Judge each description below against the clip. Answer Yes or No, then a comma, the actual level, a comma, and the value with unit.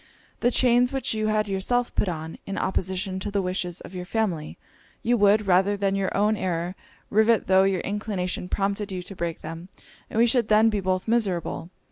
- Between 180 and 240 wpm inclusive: Yes, average, 195 wpm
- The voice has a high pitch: Yes, high, 195 Hz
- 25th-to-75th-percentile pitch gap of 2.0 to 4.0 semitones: Yes, average, 2.9 semitones